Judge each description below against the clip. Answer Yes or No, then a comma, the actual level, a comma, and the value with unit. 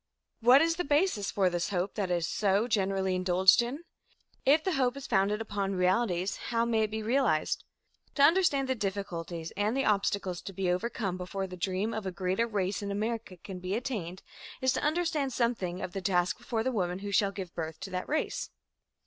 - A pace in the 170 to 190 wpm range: No, average, 200 wpm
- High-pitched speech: Yes, high, 200 Hz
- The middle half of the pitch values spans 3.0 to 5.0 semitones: Yes, average, 4.5 semitones